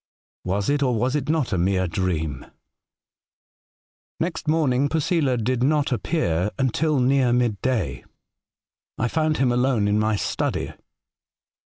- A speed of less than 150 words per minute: Yes, slow, 135 wpm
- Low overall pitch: Yes, low, 125 Hz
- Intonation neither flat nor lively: No, wide, 5.8 semitones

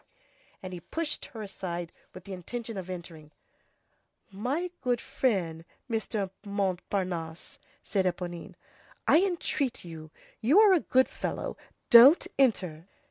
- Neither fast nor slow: No, slow, 125 wpm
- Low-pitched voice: No, high, 195 Hz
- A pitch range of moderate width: No, wide, 6.4 semitones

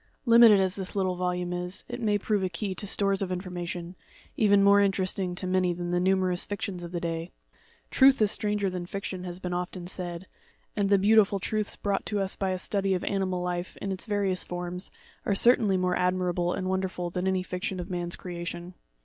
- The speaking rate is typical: No, fast, 210 wpm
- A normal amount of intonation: No, narrow, 2.0 semitones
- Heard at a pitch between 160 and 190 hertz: Yes, medium, 185 Hz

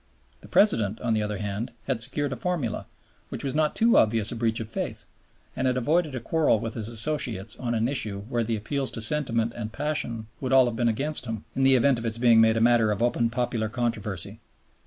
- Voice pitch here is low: Yes, low, 115 Hz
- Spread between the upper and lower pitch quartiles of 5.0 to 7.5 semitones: No, average, 3.1 semitones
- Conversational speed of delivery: No, fast, 225 wpm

